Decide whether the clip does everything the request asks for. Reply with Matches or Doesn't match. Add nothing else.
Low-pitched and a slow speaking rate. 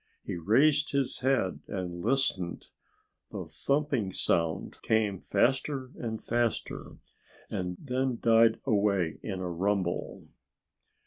Matches